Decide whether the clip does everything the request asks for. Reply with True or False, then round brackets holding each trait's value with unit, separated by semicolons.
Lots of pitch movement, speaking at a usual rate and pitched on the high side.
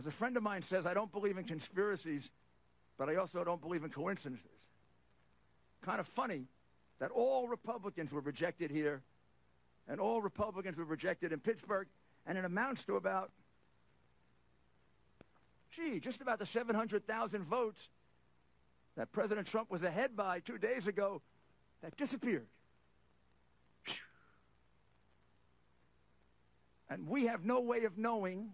False (6.1 semitones; 130 wpm; 195 Hz)